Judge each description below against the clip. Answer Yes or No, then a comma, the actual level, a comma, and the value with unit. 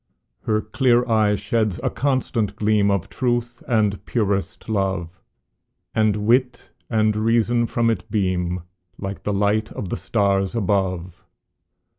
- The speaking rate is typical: No, slow, 130 wpm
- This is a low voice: Yes, low, 105 Hz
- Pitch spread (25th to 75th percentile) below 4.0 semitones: Yes, average, 2.8 semitones